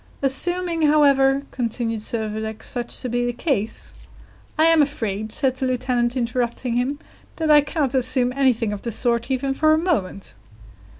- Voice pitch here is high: Yes, very high, 255 Hz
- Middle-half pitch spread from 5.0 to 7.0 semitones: No, average, 3.3 semitones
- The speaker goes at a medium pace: Yes, average, 165 wpm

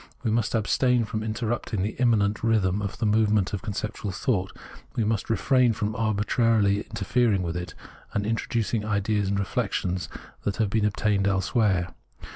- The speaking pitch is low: Yes, low, 105 Hz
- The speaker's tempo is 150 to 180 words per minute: Yes, average, 160 wpm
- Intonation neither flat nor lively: No, narrow, 2.1 semitones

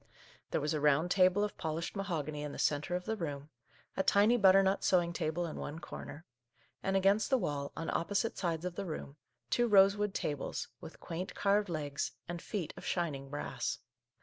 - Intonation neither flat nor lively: Yes, average, 4.4 semitones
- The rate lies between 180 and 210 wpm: Yes, average, 185 wpm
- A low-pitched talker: No, medium, 175 Hz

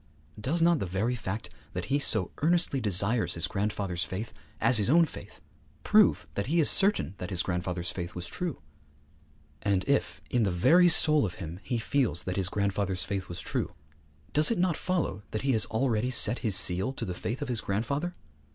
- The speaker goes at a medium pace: Yes, average, 195 wpm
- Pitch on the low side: Yes, low, 110 Hz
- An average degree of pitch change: No, wide, 7.1 semitones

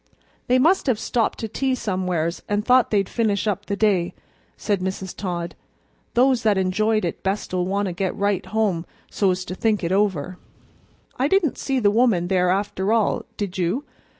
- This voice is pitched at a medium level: No, high, 200 Hz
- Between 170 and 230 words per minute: Yes, average, 180 wpm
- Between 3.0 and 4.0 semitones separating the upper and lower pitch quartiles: Yes, average, 3.3 semitones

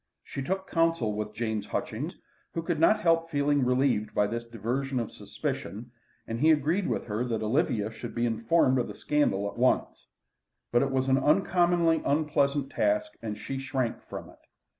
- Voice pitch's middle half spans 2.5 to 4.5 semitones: No, wide, 5.4 semitones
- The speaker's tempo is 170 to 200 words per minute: Yes, average, 180 wpm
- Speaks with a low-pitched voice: Yes, low, 130 Hz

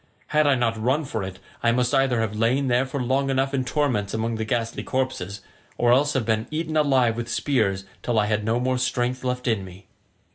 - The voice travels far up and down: No, average, 3.0 semitones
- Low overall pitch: Yes, low, 120 Hz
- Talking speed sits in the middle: No, fast, 215 wpm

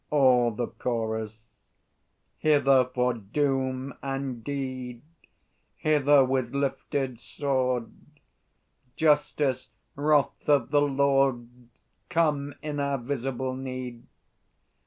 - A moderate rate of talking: No, slow, 90 wpm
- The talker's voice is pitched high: No, low, 135 Hz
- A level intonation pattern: Yes, narrow, 2.3 semitones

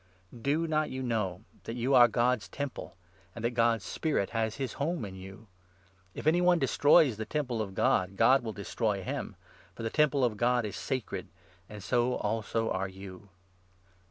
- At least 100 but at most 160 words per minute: No, average, 185 wpm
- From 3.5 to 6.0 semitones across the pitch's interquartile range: Yes, average, 4.4 semitones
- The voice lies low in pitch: Yes, low, 115 Hz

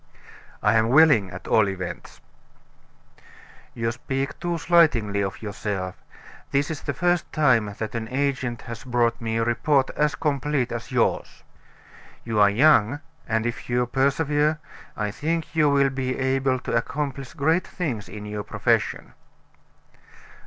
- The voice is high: No, low, 130 Hz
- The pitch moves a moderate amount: Yes, average, 4.6 semitones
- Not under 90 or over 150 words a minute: Yes, average, 145 wpm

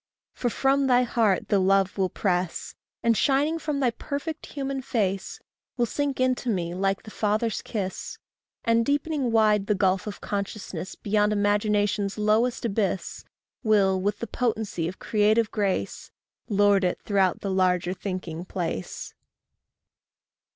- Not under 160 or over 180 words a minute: No, average, 140 wpm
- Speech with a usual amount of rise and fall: Yes, average, 3.7 semitones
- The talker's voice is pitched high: Yes, high, 210 Hz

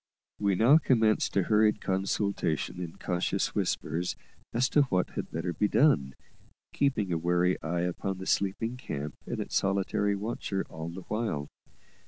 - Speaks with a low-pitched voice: Yes, very low, 95 Hz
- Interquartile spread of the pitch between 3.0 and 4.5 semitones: Yes, average, 3.7 semitones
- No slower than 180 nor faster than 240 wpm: No, average, 155 wpm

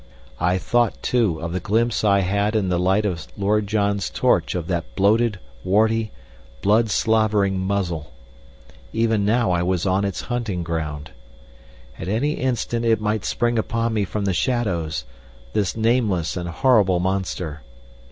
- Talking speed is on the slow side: No, average, 150 wpm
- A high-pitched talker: No, low, 100 Hz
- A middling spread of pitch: Yes, average, 3.7 semitones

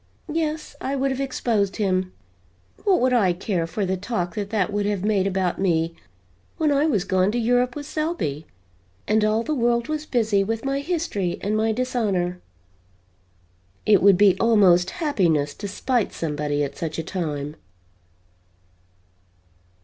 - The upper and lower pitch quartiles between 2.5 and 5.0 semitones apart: No, wide, 5.6 semitones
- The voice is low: No, high, 205 Hz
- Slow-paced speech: No, average, 155 wpm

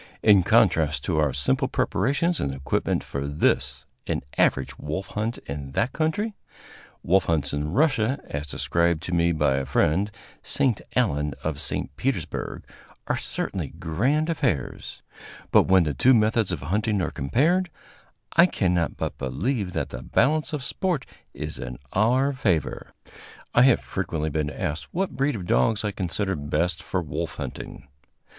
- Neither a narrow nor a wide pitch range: No, wide, 8.9 semitones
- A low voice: Yes, very low, 90 Hz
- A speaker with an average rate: Yes, average, 155 wpm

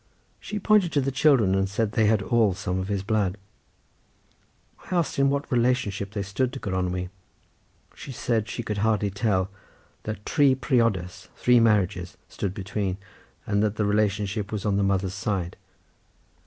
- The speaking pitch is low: Yes, low, 105 Hz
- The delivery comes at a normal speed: Yes, average, 165 wpm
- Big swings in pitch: No, average, 3.5 semitones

